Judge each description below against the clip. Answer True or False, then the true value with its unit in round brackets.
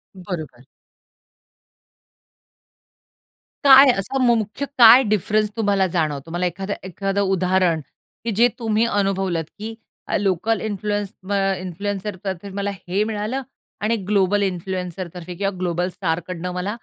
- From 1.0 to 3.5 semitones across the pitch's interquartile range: True (2.7 semitones)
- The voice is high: True (195 Hz)